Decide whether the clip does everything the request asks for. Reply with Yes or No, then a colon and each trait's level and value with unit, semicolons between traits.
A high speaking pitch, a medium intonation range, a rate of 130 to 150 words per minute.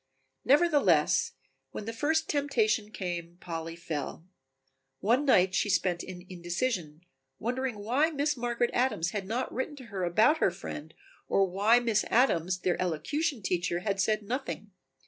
No: high, 210 Hz; wide, 6.3 semitones; average, 145 wpm